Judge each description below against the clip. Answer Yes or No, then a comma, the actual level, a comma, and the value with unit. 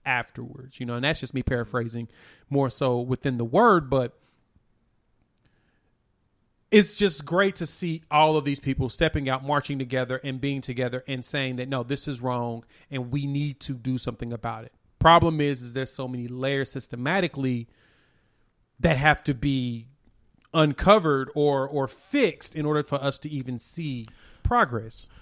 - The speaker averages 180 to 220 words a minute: No, average, 165 wpm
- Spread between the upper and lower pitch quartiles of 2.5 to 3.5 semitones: Yes, average, 3.1 semitones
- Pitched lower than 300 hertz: Yes, low, 135 Hz